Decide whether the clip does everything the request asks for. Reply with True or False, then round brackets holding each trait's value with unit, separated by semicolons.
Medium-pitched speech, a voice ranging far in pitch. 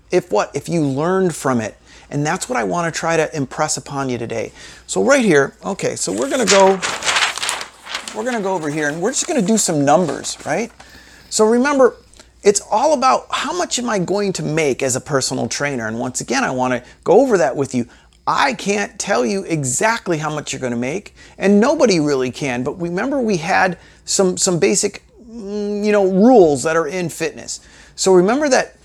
True (180 Hz; 6.6 semitones)